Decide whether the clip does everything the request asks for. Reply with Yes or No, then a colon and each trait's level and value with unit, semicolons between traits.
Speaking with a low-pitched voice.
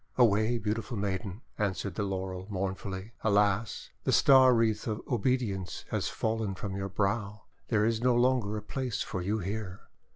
Yes: low, 105 Hz